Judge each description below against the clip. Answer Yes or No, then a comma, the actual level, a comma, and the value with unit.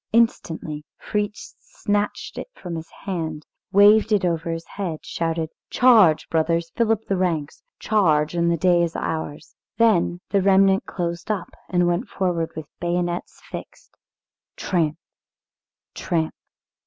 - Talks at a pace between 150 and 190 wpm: No, slow, 135 wpm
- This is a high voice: No, medium, 175 Hz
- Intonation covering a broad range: No, average, 3.4 semitones